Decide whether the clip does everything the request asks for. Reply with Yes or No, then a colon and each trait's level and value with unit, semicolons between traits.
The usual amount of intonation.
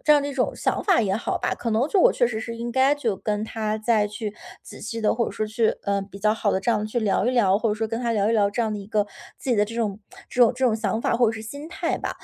No: narrow, 2.2 semitones